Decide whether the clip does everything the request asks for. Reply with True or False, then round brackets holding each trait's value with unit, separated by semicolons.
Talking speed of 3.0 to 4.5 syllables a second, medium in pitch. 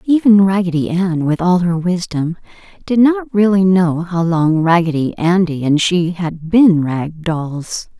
True (4.0 syllables/s; 175 Hz)